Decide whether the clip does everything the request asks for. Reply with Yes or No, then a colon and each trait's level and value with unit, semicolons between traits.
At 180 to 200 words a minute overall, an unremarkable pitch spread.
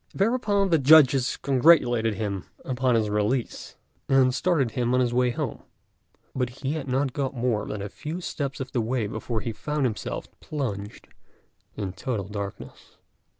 No: average, 160 wpm; average, 4.0 semitones